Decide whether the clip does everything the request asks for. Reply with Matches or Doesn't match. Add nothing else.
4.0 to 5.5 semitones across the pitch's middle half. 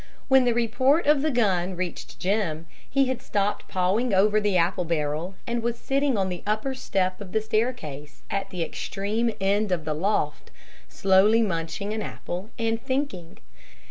Matches